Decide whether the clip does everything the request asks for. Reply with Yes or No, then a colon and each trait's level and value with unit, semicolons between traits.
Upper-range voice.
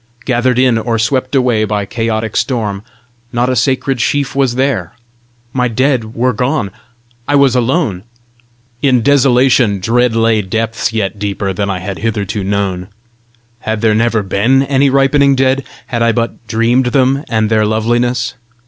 No: low, 115 Hz